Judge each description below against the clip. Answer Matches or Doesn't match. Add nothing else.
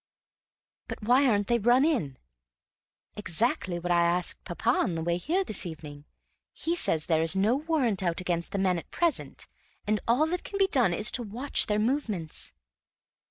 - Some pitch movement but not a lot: Doesn't match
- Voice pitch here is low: Doesn't match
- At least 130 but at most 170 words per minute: Doesn't match